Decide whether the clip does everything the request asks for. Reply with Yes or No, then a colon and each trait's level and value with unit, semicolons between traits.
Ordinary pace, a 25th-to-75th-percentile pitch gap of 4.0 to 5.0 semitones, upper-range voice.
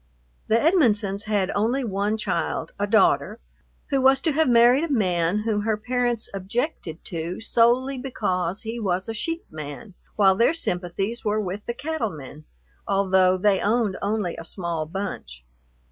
Yes: average, 160 wpm; average, 4.3 semitones; high, 210 Hz